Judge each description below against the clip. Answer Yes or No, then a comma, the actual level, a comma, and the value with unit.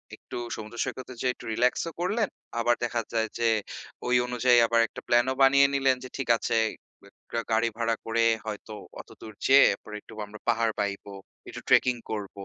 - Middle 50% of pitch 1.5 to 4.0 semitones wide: Yes, narrow, 2.4 semitones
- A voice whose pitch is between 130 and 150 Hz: No, low, 115 Hz